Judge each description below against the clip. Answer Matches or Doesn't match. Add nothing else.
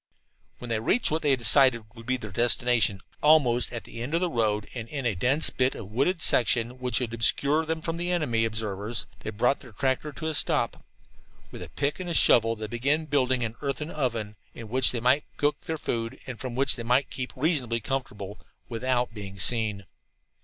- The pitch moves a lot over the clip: Doesn't match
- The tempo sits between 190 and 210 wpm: Matches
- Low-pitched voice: Matches